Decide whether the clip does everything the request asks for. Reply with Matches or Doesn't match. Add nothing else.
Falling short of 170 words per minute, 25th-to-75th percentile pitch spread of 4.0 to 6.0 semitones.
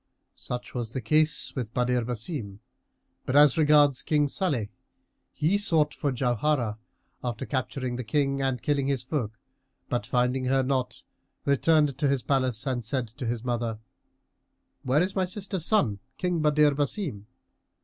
Doesn't match